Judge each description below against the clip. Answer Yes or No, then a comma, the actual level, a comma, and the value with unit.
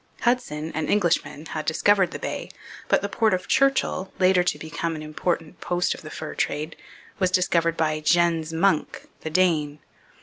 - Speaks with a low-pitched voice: No, medium, 170 Hz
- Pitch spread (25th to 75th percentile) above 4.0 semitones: No, average, 3.0 semitones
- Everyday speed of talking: Yes, average, 170 wpm